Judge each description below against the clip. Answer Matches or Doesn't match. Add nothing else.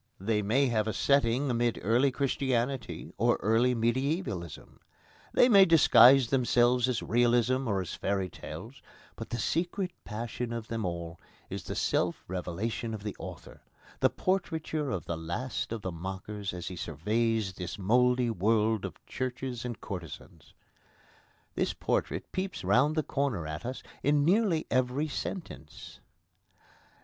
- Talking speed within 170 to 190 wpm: Doesn't match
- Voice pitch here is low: Matches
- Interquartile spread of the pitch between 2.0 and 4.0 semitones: Doesn't match